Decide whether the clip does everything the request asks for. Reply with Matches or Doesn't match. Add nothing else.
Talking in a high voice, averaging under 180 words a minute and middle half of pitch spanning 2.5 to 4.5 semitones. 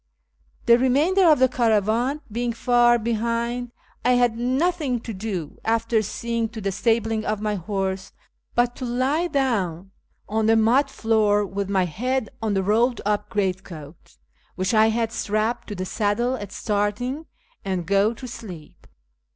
Matches